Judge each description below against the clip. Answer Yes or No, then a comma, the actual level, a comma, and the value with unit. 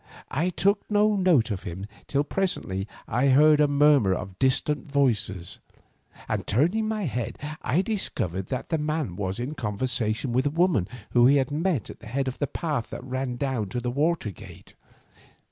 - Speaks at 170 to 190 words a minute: Yes, average, 180 wpm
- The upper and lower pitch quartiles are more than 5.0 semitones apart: Yes, wide, 5.6 semitones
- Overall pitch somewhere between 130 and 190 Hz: Yes, low, 135 Hz